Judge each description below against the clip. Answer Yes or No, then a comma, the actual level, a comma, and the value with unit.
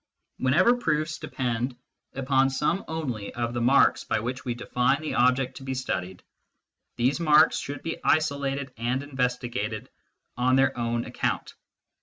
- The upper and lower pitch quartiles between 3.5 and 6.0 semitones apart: No, average, 2.8 semitones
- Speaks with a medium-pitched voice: No, low, 130 Hz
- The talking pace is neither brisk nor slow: Yes, average, 145 wpm